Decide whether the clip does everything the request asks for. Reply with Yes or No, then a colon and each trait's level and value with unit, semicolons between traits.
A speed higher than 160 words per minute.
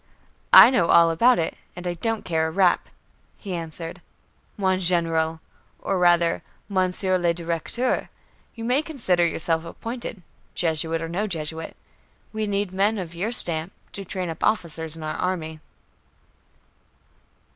No: average, 145 wpm